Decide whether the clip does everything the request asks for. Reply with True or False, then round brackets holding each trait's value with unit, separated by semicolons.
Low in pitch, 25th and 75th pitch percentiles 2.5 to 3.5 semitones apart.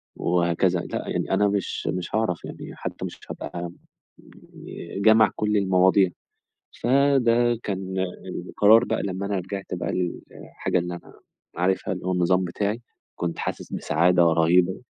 True (95 Hz; 2.8 semitones)